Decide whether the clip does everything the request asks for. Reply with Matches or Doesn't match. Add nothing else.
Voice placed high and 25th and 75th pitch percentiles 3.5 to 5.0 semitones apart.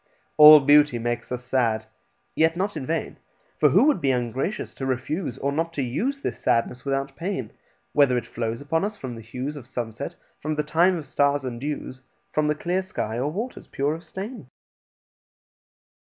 Doesn't match